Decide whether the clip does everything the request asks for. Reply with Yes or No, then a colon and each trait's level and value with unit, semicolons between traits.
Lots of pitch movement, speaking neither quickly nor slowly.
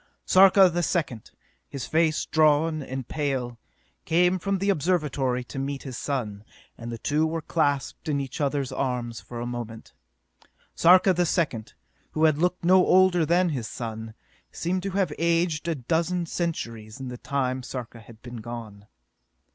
Yes: wide, 5.7 semitones; average, 165 wpm